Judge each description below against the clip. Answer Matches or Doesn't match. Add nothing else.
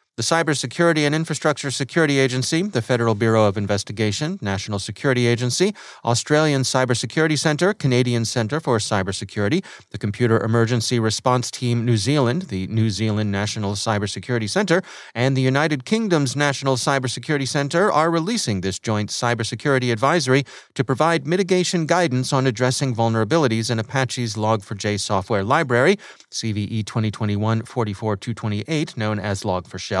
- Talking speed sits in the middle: Doesn't match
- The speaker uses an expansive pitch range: Doesn't match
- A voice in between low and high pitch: Doesn't match